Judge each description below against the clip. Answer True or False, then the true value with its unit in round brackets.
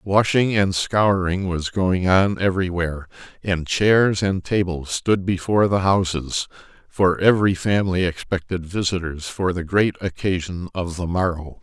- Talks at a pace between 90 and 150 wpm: True (135 wpm)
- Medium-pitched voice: False (90 Hz)